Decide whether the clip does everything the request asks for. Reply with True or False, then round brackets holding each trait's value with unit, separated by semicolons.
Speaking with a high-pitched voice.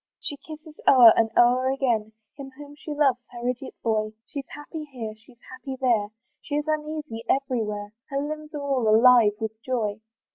True (255 Hz)